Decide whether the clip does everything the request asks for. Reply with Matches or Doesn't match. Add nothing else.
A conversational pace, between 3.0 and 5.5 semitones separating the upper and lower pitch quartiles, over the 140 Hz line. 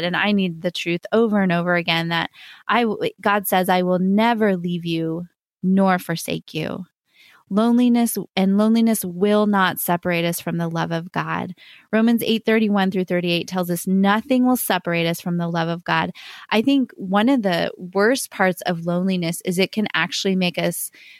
Matches